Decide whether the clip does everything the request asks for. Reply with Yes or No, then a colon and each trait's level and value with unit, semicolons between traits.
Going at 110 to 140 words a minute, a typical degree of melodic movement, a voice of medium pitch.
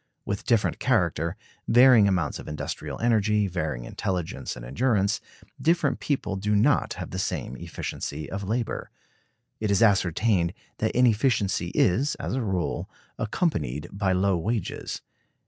No: slow, 135 wpm; average, 4.5 semitones; low, 100 Hz